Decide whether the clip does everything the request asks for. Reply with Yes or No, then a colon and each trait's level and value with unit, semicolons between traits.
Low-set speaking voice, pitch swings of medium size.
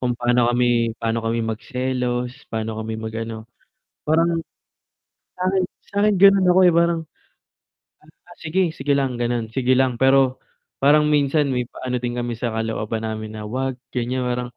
Yes: low, 125 Hz; average, 4.1 semitones